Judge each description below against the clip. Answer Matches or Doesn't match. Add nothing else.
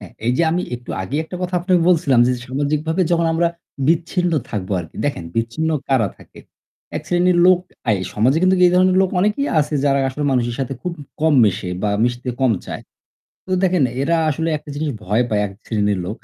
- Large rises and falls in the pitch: Matches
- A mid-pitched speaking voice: Matches